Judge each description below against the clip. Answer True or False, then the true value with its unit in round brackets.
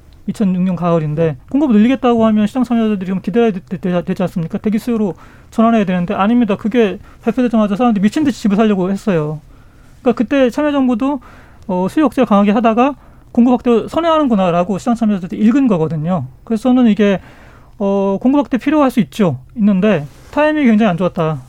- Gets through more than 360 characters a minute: True (415 characters per minute)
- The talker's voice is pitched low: False (215 Hz)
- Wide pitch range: False (4.7 semitones)